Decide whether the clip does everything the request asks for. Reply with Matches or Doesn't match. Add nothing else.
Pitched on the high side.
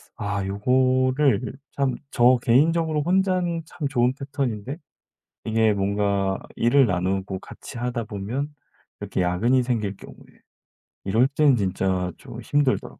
Doesn't match